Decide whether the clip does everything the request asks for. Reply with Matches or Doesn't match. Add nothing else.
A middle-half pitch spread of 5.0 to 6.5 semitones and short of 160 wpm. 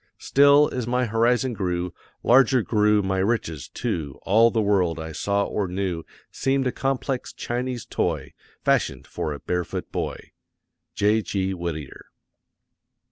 Matches